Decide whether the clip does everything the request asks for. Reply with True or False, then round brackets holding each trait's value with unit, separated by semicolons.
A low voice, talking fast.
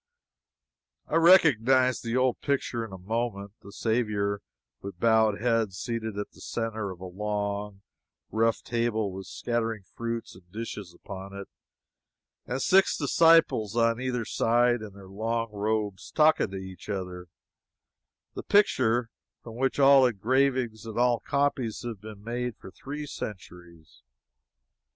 False (115 Hz; 140 wpm)